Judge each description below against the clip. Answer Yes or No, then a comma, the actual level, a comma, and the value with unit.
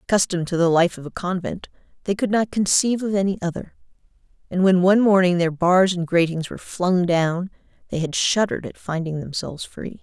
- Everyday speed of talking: Yes, average, 190 wpm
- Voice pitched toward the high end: No, medium, 180 Hz